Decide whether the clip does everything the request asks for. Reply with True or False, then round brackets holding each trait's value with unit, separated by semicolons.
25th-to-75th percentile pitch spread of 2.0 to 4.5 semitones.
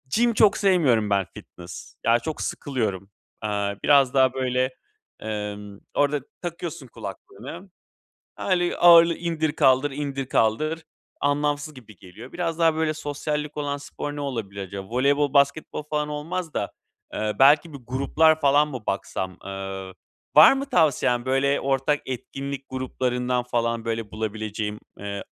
False (5.3 semitones)